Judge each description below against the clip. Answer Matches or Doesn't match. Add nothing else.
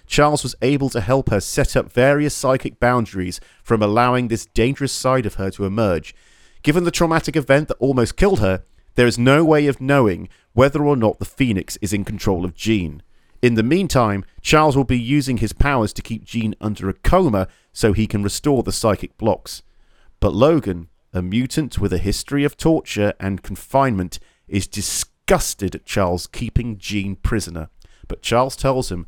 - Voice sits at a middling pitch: Doesn't match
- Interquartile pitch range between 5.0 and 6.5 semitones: Matches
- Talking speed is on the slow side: Doesn't match